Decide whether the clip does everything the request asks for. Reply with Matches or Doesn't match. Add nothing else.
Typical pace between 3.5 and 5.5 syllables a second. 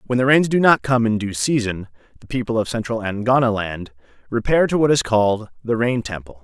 Doesn't match